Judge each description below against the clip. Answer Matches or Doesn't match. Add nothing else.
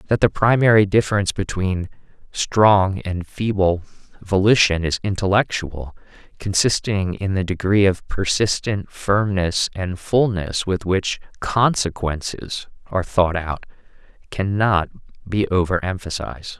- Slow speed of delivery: Matches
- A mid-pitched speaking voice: Doesn't match